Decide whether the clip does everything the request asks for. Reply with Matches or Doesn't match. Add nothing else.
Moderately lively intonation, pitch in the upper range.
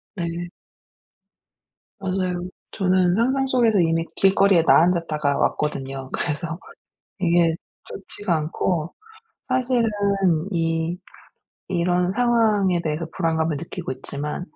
Doesn't match